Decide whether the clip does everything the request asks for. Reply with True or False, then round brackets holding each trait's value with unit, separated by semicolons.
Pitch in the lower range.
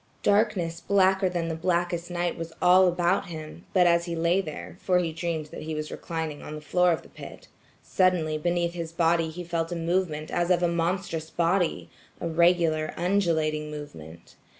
False (170 Hz)